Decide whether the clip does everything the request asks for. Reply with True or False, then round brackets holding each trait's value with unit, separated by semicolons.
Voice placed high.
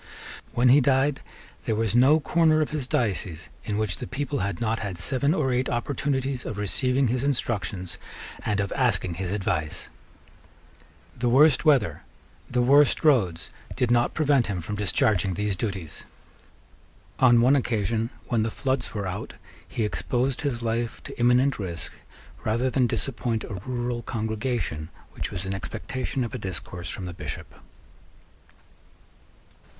False (120 Hz)